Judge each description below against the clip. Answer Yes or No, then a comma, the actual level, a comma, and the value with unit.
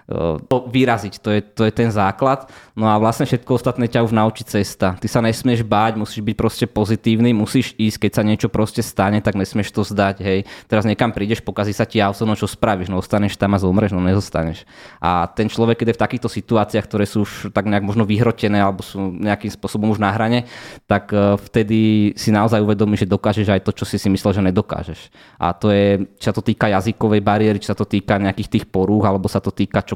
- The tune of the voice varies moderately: No, narrow, 2.0 semitones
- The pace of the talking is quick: Yes, fast, 225 wpm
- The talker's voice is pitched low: Yes, low, 105 Hz